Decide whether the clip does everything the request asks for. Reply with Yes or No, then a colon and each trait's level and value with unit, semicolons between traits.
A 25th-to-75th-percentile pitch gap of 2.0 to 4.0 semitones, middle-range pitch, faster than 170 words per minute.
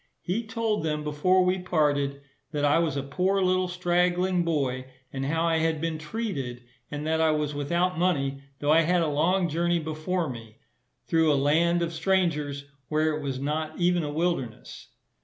Yes: average, 3.4 semitones; medium, 160 Hz; average, 180 wpm